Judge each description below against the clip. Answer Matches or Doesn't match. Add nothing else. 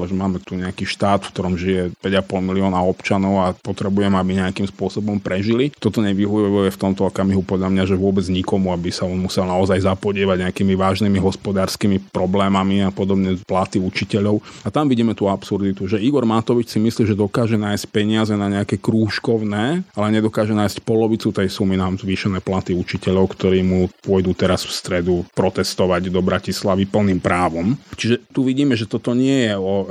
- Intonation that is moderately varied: Doesn't match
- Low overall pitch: Matches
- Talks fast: Matches